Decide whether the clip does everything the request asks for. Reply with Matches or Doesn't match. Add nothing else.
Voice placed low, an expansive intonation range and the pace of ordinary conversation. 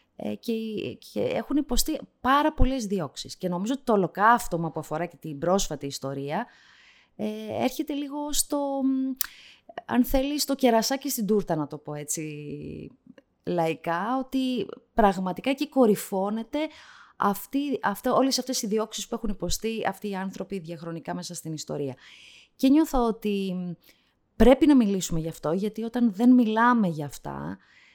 Doesn't match